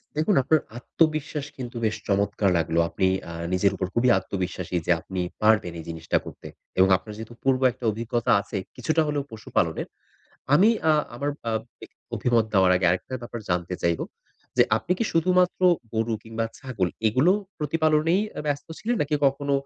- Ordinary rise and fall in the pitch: No, wide, 7.5 semitones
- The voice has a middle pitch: No, low, 115 Hz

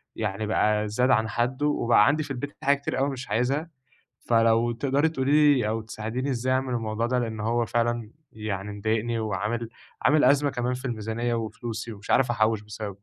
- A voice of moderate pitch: No, low, 120 Hz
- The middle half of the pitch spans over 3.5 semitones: No, average, 3.1 semitones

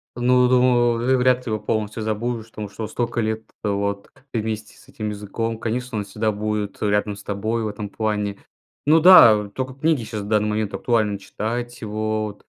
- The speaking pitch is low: Yes, low, 110 Hz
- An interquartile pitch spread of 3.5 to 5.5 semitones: No, narrow, 2.5 semitones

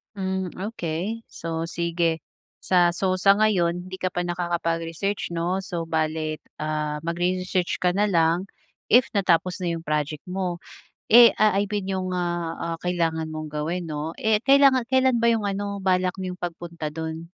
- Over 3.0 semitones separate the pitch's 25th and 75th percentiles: No, average, 2.7 semitones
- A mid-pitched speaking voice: Yes, medium, 175 Hz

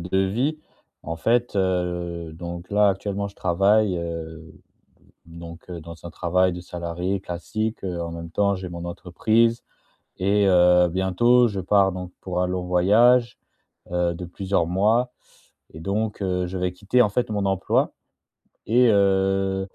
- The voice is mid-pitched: No, very low, 95 Hz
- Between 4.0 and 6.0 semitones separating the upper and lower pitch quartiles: No, average, 2.7 semitones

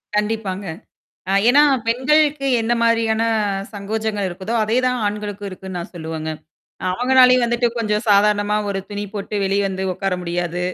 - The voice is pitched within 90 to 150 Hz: No, high, 210 Hz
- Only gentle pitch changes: No, average, 3.4 semitones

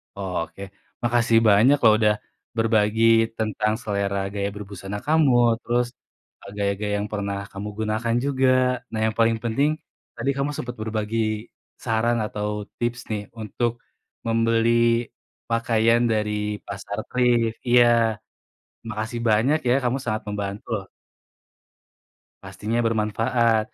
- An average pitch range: No, narrow, 2.1 semitones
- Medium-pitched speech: No, low, 110 Hz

